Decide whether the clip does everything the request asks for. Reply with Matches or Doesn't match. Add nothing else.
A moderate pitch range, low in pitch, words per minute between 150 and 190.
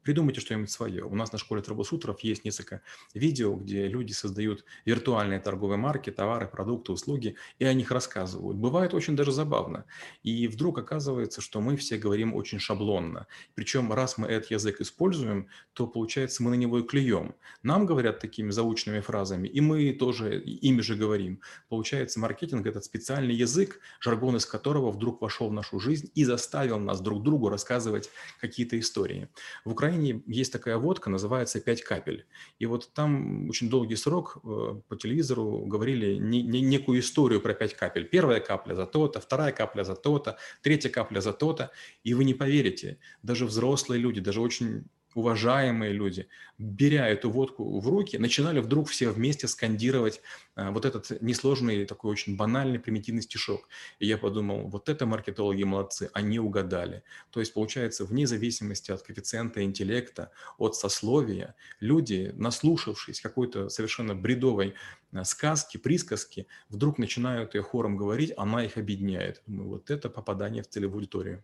Matches